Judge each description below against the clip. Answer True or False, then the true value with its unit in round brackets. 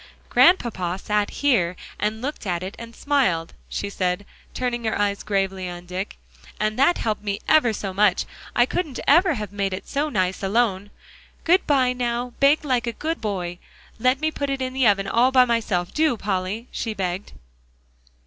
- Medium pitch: False (220 Hz)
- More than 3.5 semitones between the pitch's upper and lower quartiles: True (5.1 semitones)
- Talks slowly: False (175 wpm)